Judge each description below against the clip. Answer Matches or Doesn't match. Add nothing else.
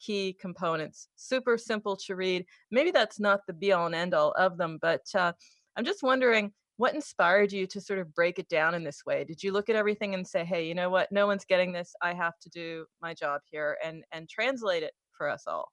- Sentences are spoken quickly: Matches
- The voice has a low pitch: Doesn't match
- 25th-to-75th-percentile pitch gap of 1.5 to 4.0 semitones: Matches